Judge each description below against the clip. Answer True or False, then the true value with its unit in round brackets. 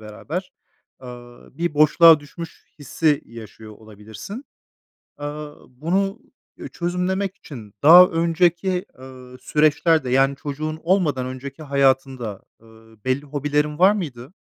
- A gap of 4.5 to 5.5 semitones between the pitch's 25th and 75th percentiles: True (5.0 semitones)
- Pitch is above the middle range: False (145 Hz)